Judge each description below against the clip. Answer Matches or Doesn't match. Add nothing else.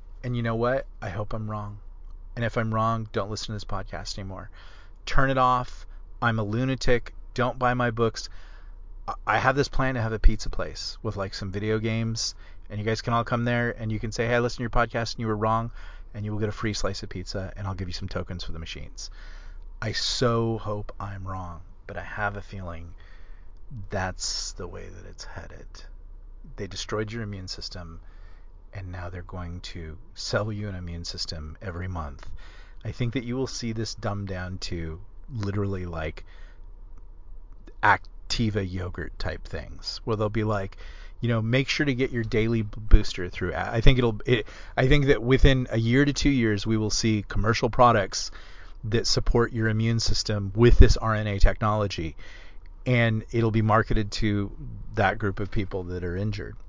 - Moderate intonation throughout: Matches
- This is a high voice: Doesn't match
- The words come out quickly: Doesn't match